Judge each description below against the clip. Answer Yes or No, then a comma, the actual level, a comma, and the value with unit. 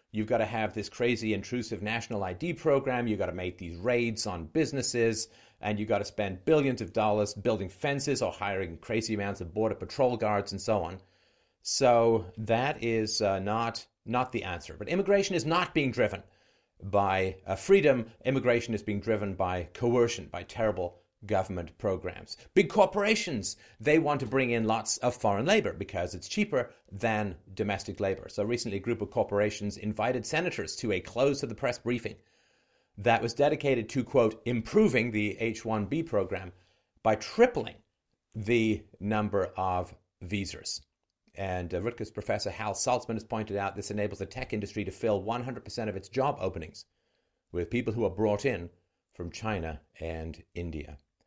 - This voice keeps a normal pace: Yes, average, 170 wpm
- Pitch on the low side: Yes, low, 110 Hz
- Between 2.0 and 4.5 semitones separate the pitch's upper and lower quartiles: Yes, average, 3.7 semitones